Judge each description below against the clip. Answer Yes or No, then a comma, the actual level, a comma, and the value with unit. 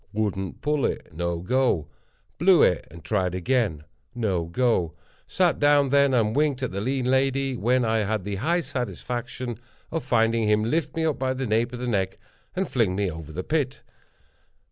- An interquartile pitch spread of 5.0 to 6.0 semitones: Yes, wide, 5.6 semitones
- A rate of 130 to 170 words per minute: No, average, 180 wpm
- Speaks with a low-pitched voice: Yes, low, 120 Hz